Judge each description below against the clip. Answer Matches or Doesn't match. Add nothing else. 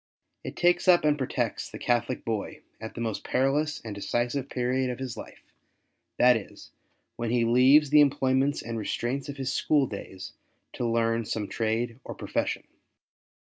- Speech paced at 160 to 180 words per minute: Matches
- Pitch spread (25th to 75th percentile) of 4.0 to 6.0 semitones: Doesn't match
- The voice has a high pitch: Doesn't match